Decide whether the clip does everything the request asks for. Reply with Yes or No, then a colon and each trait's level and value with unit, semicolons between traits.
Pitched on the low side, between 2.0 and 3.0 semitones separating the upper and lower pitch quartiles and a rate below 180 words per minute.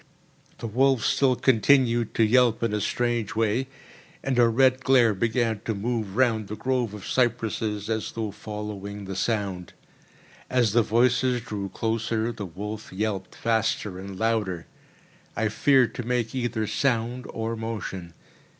Yes: low, 115 Hz; narrow, 2.6 semitones; average, 150 wpm